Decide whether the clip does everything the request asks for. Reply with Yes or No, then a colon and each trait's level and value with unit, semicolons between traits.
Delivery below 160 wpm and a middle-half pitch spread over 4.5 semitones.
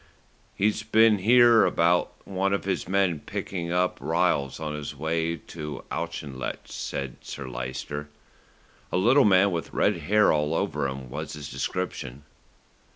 Yes: average, 145 wpm; average, 4.9 semitones